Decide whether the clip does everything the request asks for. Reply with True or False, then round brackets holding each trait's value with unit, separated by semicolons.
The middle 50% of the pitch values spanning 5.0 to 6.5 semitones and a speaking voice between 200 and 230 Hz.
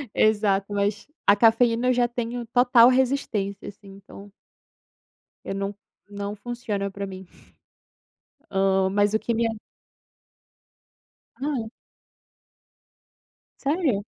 False (3.4 semitones; 210 Hz)